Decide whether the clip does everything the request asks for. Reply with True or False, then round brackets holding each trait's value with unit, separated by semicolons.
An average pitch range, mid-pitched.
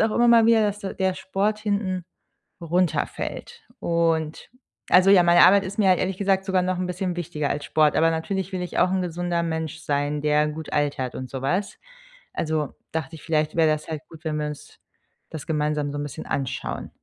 True (3.8 semitones; 170 Hz)